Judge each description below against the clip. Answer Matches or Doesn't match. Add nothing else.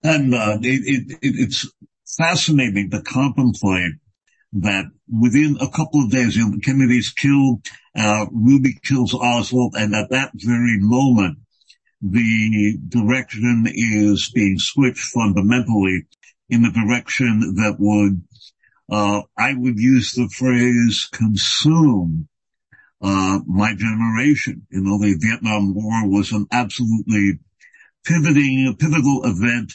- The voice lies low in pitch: Matches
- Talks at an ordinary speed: Doesn't match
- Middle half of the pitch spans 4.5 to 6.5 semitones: Doesn't match